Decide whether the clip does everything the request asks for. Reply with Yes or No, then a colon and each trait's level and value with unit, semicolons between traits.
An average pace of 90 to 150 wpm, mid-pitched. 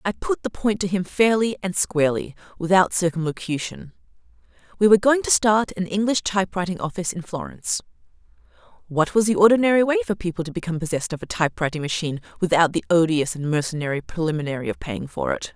No: average, 175 wpm; medium, 180 Hz